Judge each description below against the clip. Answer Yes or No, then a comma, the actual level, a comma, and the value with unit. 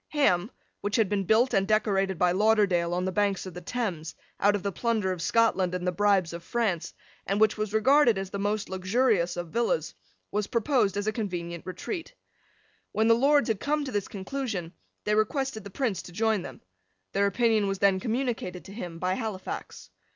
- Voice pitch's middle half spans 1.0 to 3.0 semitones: No, average, 3.5 semitones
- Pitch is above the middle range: Yes, high, 205 Hz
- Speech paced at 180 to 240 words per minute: Yes, average, 195 wpm